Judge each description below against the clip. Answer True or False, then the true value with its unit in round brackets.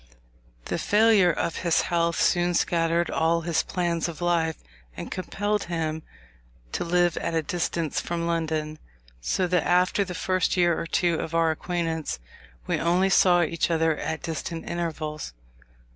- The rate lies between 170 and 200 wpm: False (155 wpm)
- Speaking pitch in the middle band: True (170 Hz)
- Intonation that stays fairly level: True (1.5 semitones)